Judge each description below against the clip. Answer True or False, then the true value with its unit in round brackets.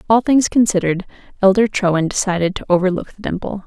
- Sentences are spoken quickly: False (165 wpm)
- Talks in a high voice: True (195 Hz)